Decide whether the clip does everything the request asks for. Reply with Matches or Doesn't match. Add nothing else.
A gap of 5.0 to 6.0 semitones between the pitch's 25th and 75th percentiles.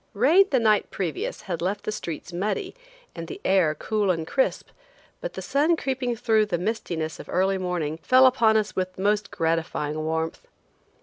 Matches